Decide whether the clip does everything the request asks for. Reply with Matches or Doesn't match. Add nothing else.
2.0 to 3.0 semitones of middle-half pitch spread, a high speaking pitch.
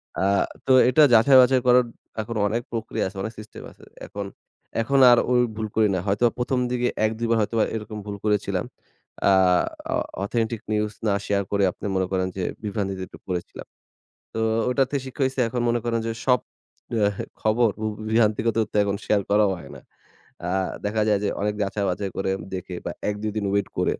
Doesn't match